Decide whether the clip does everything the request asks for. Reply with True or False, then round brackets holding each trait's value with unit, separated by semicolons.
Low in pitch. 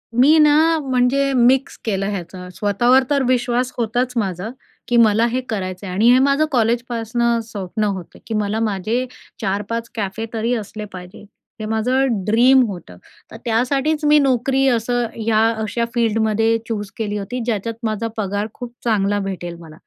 False (225 Hz)